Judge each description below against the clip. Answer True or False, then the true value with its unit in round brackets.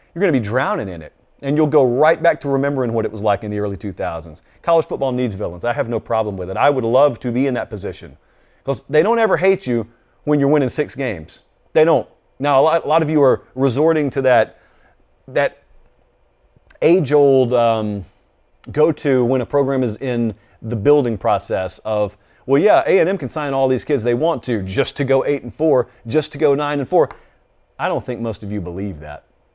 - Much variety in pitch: False (4.5 semitones)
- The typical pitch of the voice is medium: False (130 Hz)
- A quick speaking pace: True (215 wpm)